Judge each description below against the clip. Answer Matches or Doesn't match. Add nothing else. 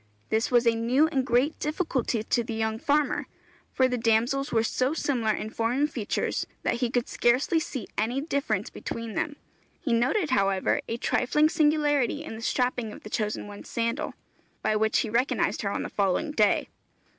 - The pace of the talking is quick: Doesn't match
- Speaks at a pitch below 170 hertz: Doesn't match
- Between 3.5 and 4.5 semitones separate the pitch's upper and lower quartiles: Matches